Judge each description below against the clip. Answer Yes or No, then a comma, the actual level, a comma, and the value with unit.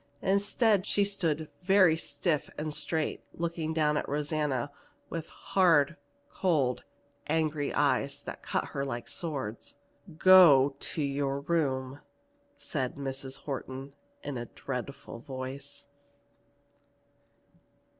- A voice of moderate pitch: Yes, medium, 145 Hz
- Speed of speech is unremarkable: No, slow, 105 wpm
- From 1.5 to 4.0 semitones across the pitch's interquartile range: Yes, average, 3.5 semitones